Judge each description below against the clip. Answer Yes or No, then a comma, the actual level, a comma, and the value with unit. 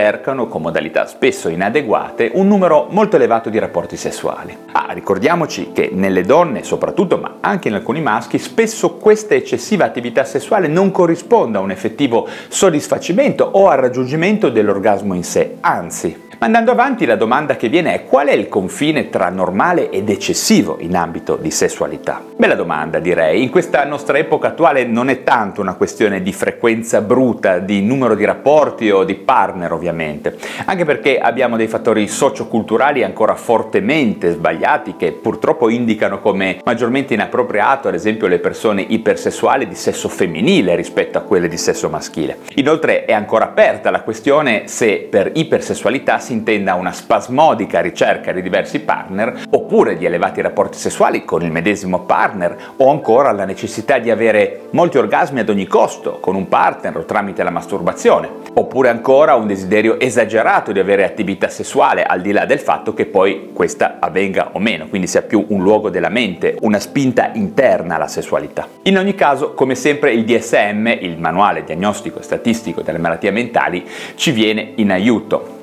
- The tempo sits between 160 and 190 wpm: Yes, average, 165 wpm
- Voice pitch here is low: No, medium, 175 Hz